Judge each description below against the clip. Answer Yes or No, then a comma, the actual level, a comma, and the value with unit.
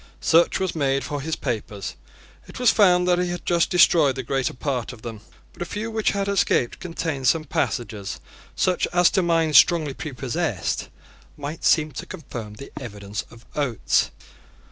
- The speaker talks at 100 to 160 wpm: No, average, 170 wpm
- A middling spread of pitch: No, wide, 6.1 semitones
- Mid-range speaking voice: Yes, medium, 150 Hz